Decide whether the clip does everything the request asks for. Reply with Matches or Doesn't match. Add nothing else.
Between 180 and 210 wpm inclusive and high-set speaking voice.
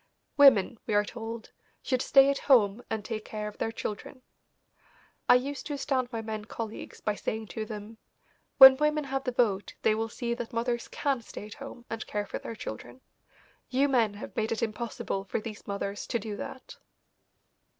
Matches